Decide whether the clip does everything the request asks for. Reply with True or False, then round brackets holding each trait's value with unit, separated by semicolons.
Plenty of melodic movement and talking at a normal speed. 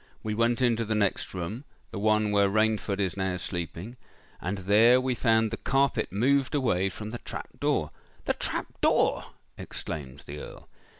False (3.7 semitones; 160 wpm)